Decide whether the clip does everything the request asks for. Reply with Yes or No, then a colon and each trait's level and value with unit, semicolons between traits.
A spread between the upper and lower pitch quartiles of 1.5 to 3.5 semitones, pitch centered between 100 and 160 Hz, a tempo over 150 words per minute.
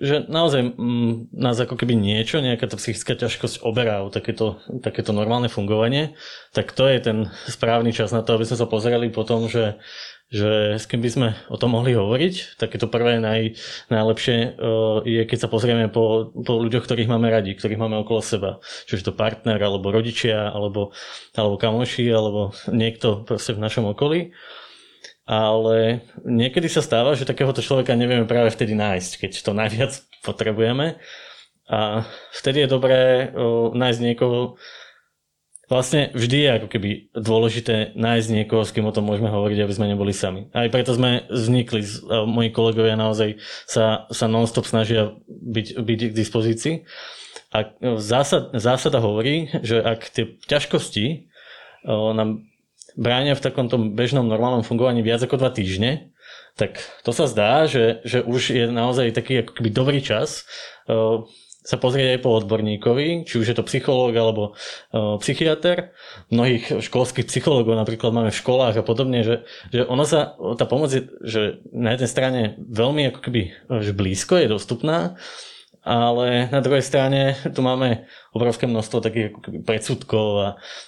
Yes: narrow, 2.4 semitones; low, 115 Hz; average, 160 wpm